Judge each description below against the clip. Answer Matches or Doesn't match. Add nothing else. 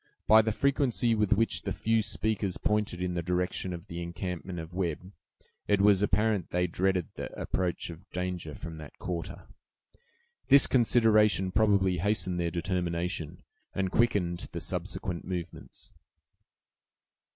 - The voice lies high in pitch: Doesn't match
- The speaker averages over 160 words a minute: Doesn't match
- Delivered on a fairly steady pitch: Doesn't match